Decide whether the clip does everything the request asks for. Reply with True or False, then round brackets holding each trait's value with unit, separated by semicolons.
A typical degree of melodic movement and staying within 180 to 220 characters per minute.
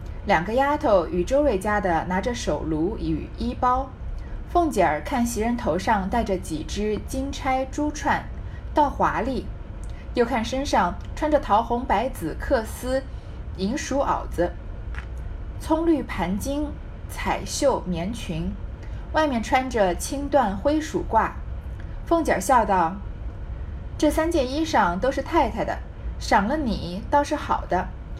False (5.9 semitones; 190 characters per minute)